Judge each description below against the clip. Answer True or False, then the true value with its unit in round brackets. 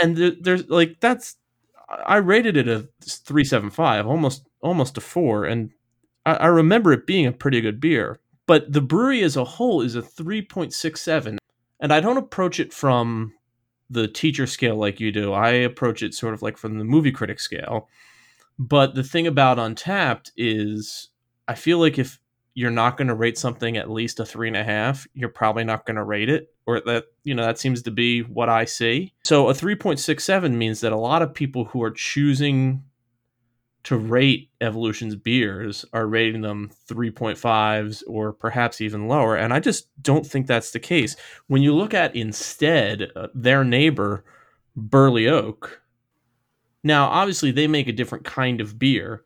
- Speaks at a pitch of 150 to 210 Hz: False (125 Hz)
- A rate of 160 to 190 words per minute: True (185 wpm)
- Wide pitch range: False (4.8 semitones)